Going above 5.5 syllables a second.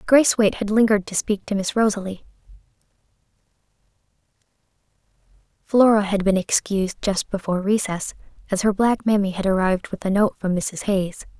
Yes: 5.8 syllables/s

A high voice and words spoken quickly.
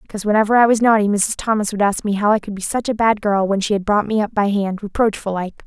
Yes: high, 210 Hz; fast, 285 wpm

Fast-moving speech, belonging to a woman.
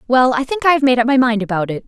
Yes: fast, 355 wpm; female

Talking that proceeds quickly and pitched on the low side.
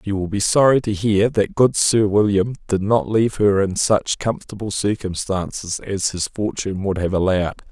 No: average, 185 wpm; low, 100 Hz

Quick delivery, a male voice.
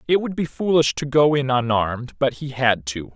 Yes: fast, 230 wpm; male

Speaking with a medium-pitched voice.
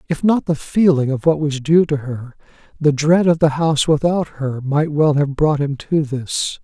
Yes: medium, 150 Hz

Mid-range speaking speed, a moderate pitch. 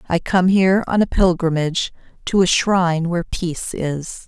Yes: average, 170 wpm; medium, 175 Hz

